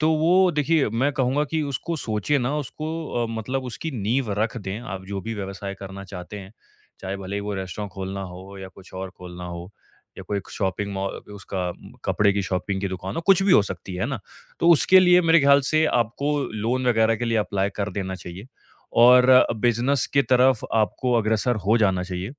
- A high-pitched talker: No, low, 110 Hz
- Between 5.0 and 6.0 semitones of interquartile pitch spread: Yes, wide, 5.5 semitones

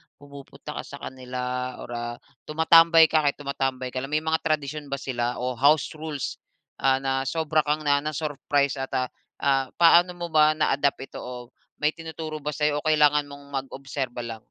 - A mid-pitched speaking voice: Yes, medium, 145 Hz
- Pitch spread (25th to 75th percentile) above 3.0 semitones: No, average, 2.7 semitones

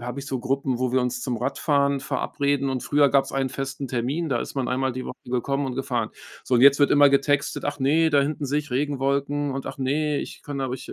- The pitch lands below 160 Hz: Yes, low, 135 Hz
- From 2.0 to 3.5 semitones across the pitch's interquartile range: No, narrow, 1.6 semitones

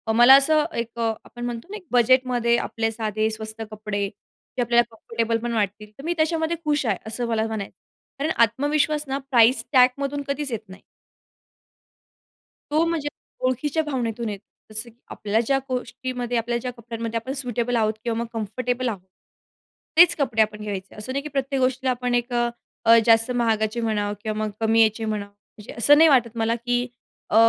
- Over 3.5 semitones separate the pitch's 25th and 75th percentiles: No, average, 2.9 semitones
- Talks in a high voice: Yes, high, 235 Hz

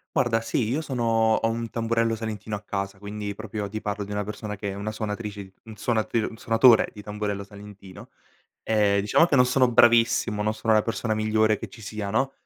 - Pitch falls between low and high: No, low, 110 Hz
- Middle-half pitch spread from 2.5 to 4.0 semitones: No, narrow, 1.8 semitones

